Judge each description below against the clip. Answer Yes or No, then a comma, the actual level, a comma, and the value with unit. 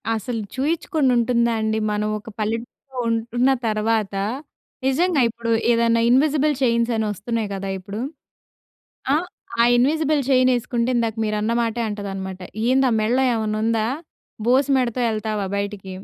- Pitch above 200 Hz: Yes, high, 230 Hz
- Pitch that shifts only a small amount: No, average, 3.0 semitones